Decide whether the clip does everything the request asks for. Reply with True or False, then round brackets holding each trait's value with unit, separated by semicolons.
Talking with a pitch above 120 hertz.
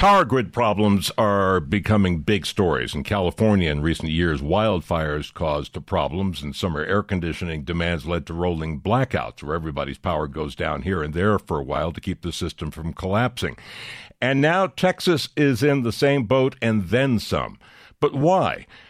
False (95 Hz)